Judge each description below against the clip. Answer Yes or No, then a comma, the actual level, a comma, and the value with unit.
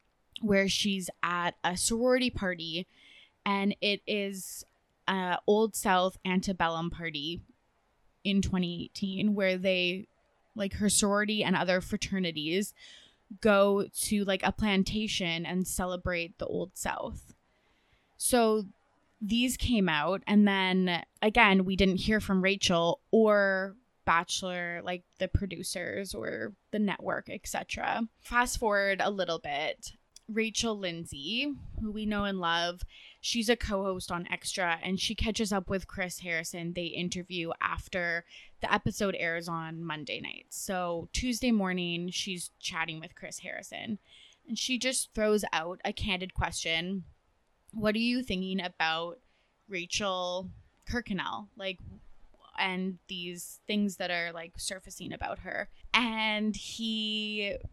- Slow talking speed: Yes, slow, 130 wpm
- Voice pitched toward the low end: No, high, 190 Hz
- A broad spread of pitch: No, average, 3.1 semitones